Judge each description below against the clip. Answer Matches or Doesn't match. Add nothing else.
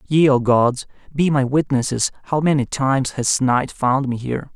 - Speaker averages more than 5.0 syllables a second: Doesn't match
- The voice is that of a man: Matches